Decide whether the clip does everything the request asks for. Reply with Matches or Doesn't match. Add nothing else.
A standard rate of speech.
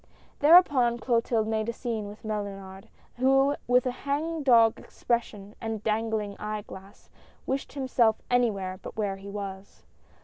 Matches